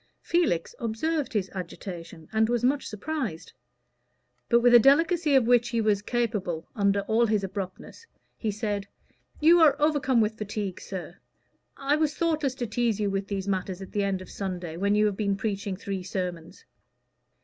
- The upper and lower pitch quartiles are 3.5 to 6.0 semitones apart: Yes, average, 4.5 semitones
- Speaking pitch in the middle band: No, high, 210 Hz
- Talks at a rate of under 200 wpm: Yes, average, 170 wpm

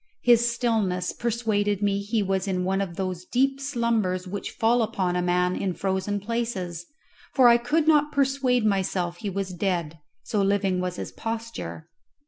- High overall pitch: Yes, high, 200 Hz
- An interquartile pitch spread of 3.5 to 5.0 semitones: Yes, average, 4.3 semitones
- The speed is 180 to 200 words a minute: No, average, 165 wpm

